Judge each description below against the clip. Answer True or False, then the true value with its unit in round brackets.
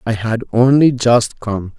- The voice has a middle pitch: False (115 Hz)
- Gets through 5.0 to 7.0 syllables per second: False (3.9 syllables/s)